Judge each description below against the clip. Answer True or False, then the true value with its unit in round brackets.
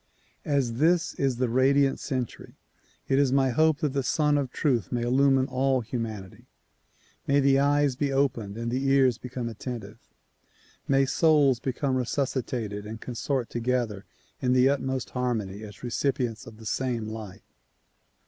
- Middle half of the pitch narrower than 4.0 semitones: True (2.9 semitones)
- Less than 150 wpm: False (155 wpm)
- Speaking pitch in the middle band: False (130 Hz)